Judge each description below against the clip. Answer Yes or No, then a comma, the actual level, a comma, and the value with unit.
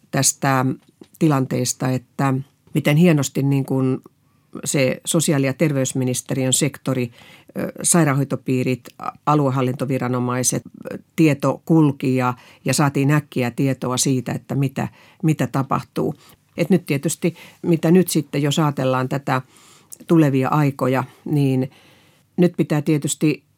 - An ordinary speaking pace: Yes, average, 105 wpm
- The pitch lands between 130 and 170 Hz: Yes, medium, 140 Hz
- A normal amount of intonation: Yes, average, 3.2 semitones